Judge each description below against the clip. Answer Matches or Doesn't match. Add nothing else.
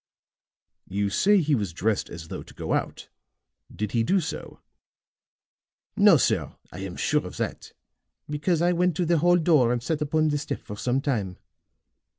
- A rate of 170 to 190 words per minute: Matches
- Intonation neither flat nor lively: Doesn't match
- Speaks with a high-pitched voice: Doesn't match